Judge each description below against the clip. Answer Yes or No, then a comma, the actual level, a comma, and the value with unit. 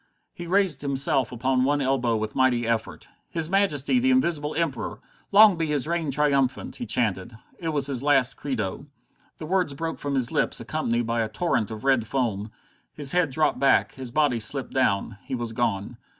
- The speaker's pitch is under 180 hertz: Yes, low, 135 Hz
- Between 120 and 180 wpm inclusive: No, average, 190 wpm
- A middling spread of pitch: Yes, average, 4.6 semitones